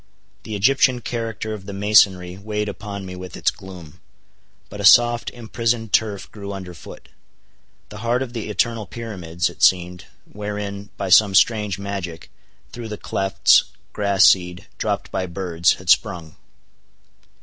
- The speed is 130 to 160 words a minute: Yes, average, 150 wpm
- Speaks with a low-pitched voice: Yes, low, 100 Hz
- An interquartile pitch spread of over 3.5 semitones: No, average, 2.9 semitones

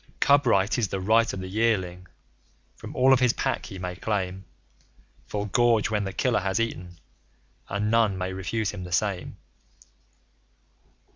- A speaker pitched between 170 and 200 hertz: No, low, 100 Hz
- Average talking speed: Yes, average, 160 wpm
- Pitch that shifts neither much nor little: Yes, average, 3.5 semitones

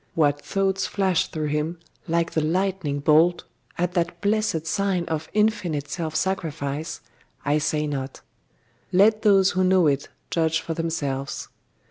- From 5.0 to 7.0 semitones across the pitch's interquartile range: No, average, 3.9 semitones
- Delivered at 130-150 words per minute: Yes, average, 140 wpm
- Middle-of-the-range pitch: Yes, medium, 165 Hz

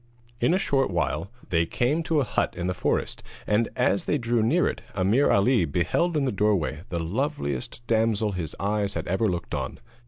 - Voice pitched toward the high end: No, low, 105 Hz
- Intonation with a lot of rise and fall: Yes, wide, 6.1 semitones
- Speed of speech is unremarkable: Yes, average, 195 wpm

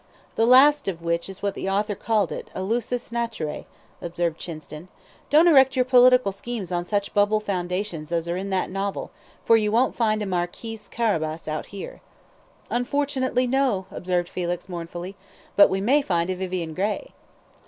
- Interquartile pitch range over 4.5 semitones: Yes, average, 5.2 semitones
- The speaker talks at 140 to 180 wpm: Yes, average, 170 wpm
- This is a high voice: Yes, high, 200 Hz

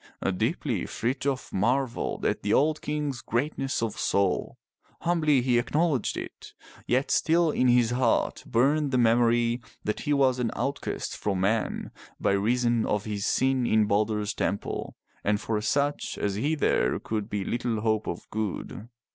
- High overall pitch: No, low, 120 Hz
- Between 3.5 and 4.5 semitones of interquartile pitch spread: Yes, average, 4.2 semitones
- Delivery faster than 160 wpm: No, average, 155 wpm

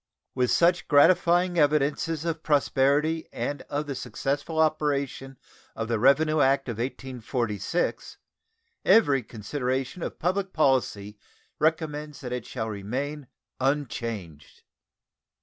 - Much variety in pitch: No, average, 3.8 semitones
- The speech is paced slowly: Yes, slow, 110 wpm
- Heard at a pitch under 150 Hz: Yes, medium, 140 Hz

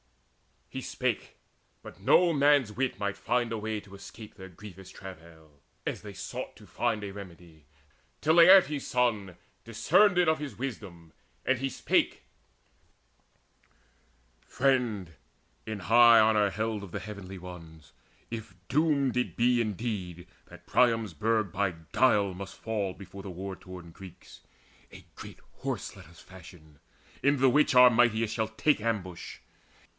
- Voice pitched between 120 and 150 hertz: No, low, 105 Hz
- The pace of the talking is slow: No, average, 145 wpm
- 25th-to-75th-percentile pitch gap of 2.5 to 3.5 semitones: No, average, 4.9 semitones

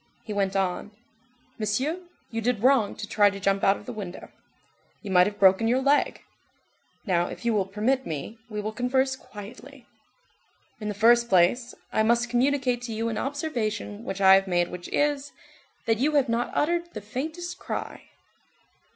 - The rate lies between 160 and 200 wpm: Yes, average, 175 wpm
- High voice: Yes, high, 225 Hz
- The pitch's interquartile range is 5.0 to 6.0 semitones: No, average, 4.5 semitones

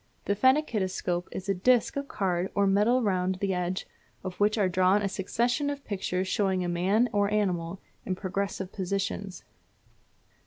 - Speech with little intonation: Yes, narrow, 2.2 semitones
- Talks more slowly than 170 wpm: Yes, average, 160 wpm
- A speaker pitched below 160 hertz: No, high, 195 Hz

